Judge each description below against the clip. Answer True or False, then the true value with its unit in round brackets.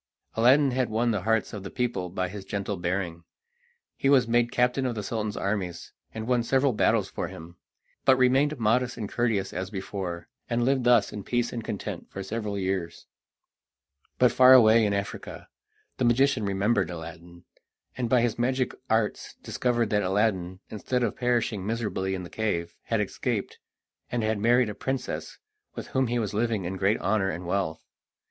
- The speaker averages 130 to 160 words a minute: False (180 wpm)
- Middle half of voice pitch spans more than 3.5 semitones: True (4.0 semitones)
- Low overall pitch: True (110 Hz)